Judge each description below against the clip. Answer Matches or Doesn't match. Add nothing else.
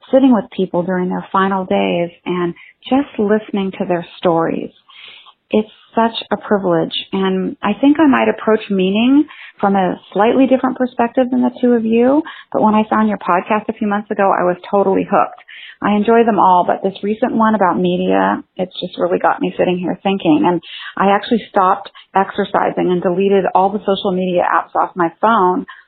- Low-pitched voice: Doesn't match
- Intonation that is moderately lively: Matches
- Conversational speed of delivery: Matches